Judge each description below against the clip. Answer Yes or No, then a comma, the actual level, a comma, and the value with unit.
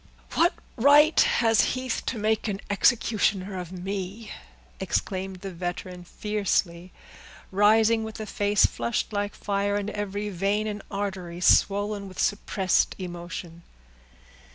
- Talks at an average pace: No, slow, 125 wpm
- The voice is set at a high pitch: Yes, high, 205 Hz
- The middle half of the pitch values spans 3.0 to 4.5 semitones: No, narrow, 2.4 semitones